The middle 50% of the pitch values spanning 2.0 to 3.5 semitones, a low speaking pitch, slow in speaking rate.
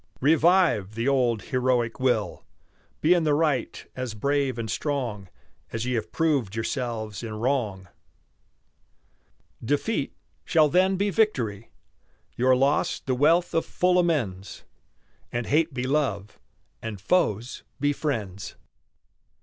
No: average, 5.3 semitones; low, 130 Hz; slow, 125 wpm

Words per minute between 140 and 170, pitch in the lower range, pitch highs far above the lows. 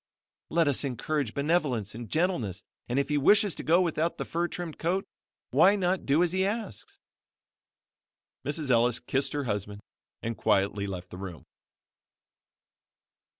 No: average, 150 wpm; medium, 145 Hz; wide, 7.8 semitones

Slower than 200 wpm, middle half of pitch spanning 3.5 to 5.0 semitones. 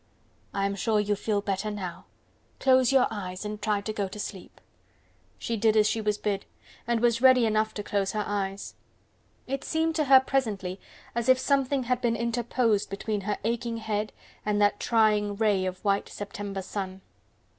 No: average, 180 wpm; average, 2.8 semitones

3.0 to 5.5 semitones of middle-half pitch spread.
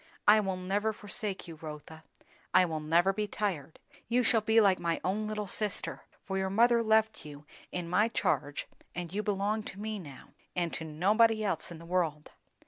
Yes: average, 4.2 semitones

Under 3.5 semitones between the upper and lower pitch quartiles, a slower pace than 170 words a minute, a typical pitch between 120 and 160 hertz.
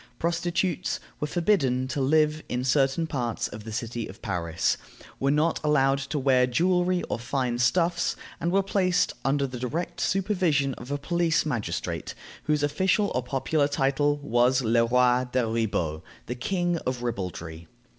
No: average, 5.2 semitones; average, 155 wpm; low, 135 Hz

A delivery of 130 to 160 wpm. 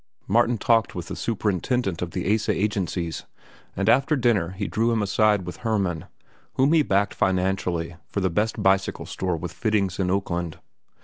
No: average, 170 wpm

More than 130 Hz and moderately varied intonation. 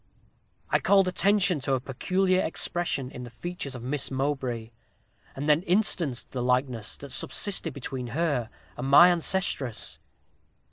No: medium, 140 Hz; wide, 5.8 semitones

